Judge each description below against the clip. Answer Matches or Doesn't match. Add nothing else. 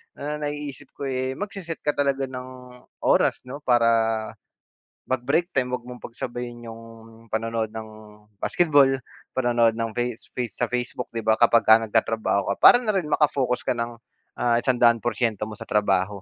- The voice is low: Matches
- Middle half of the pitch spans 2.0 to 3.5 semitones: Matches